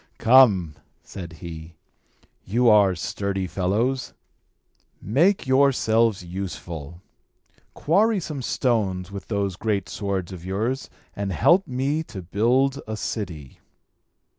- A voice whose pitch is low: Yes, low, 100 Hz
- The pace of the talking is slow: Yes, slow, 110 wpm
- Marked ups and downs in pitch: Yes, wide, 5.9 semitones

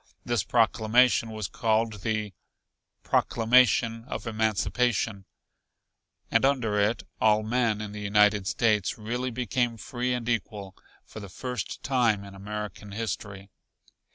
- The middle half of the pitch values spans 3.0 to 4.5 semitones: No, narrow, 2.5 semitones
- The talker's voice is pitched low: Yes, low, 110 Hz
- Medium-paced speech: No, slow, 125 wpm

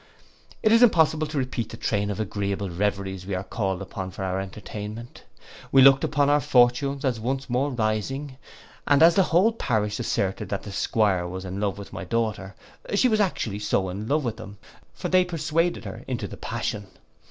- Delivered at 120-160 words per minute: No, average, 185 wpm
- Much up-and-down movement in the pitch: Yes, wide, 6.2 semitones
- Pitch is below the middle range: Yes, low, 110 Hz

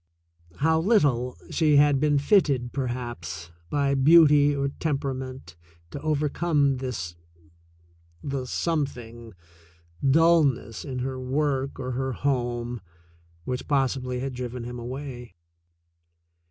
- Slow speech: Yes, slow, 120 wpm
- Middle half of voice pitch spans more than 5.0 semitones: No, average, 2.9 semitones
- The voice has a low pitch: Yes, low, 130 Hz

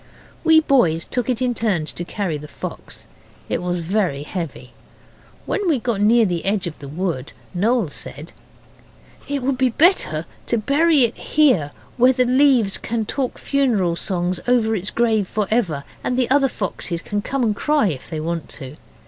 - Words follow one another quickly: No, average, 180 wpm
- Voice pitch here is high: Yes, high, 215 Hz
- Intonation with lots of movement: Yes, wide, 6.7 semitones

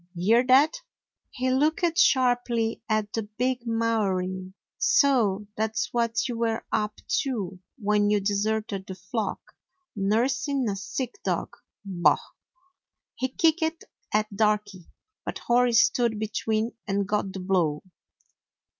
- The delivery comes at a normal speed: No, slow, 130 wpm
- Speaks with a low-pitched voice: No, high, 220 Hz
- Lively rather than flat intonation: No, average, 3.7 semitones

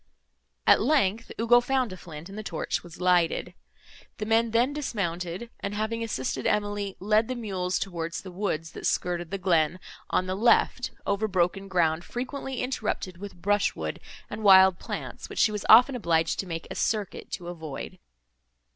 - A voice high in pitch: Yes, high, 195 Hz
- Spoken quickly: No, average, 175 wpm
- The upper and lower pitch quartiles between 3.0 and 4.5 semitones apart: Yes, average, 4.0 semitones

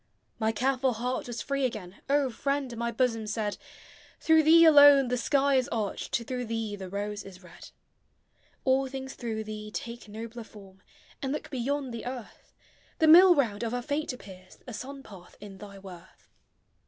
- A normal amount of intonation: Yes, average, 4.4 semitones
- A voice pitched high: Yes, high, 240 Hz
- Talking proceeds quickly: No, average, 175 wpm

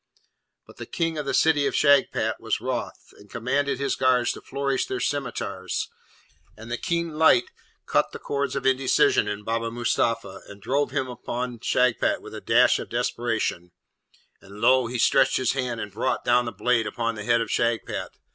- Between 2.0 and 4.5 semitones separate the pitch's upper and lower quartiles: Yes, average, 3.1 semitones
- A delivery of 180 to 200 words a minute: Yes, average, 185 wpm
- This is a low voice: Yes, low, 125 Hz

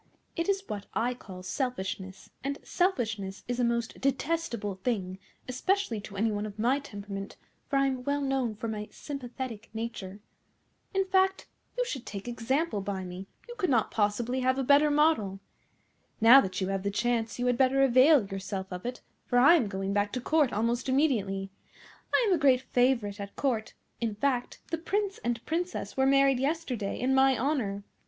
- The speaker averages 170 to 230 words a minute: Yes, average, 185 wpm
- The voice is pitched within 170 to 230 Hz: No, high, 245 Hz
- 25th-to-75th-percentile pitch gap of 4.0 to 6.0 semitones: Yes, average, 5.2 semitones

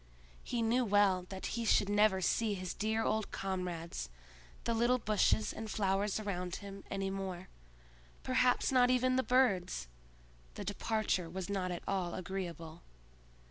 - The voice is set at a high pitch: Yes, high, 200 Hz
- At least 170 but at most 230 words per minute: No, average, 145 wpm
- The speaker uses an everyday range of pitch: Yes, average, 3.3 semitones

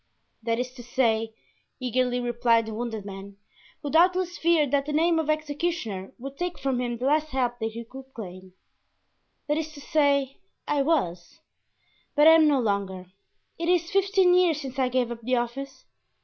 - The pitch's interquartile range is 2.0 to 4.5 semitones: No, average, 5.0 semitones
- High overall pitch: Yes, very high, 260 Hz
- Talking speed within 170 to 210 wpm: Yes, average, 175 wpm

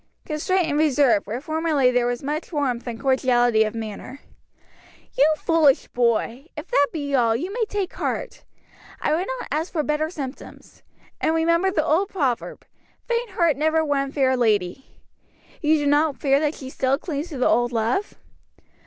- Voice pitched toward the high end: Yes, very high, 290 Hz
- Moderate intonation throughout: Yes, average, 4.2 semitones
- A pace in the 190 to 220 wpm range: No, average, 170 wpm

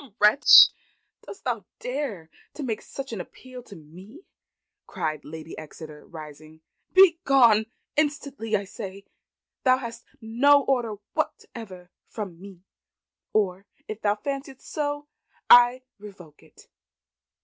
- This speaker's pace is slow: Yes, slow, 115 wpm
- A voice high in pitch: Yes, high, 220 Hz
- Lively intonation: Yes, wide, 6.6 semitones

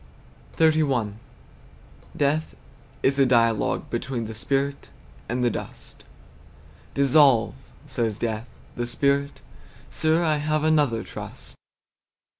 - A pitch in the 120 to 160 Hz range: Yes, low, 135 Hz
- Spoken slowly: Yes, slow, 100 wpm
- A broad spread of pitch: No, average, 4.2 semitones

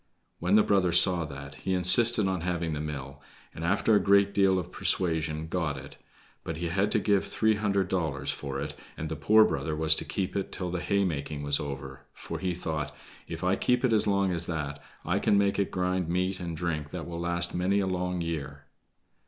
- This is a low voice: Yes, very low, 85 Hz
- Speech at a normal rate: No, fast, 215 wpm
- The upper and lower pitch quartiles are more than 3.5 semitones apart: Yes, average, 4.0 semitones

